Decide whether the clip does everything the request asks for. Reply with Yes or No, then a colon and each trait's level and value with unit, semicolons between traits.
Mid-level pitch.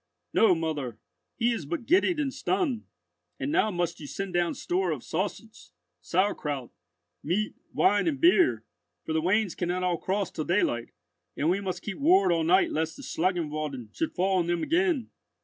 Yes: medium, 180 Hz